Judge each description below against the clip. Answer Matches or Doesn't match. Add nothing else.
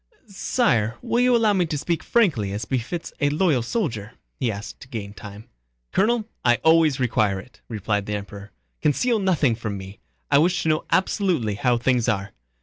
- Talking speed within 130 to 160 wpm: Doesn't match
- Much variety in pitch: Matches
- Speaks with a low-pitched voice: Matches